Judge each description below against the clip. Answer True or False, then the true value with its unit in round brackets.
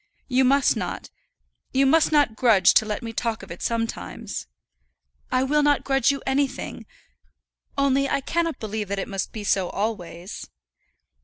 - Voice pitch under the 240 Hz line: False (245 Hz)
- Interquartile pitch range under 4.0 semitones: False (4.9 semitones)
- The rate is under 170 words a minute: True (160 wpm)